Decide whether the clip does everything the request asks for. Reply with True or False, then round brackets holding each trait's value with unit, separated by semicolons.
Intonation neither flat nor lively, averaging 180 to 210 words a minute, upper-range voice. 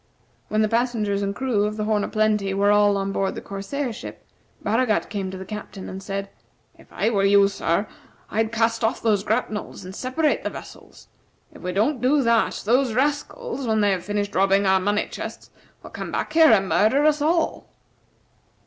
True (3.4 semitones; 195 wpm; 210 Hz)